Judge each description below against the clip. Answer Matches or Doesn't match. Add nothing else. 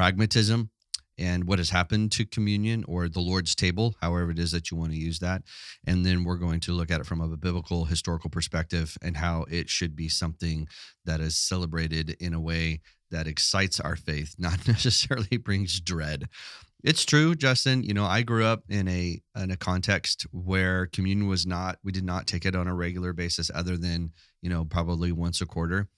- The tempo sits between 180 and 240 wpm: Matches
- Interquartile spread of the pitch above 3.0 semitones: Doesn't match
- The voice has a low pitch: Matches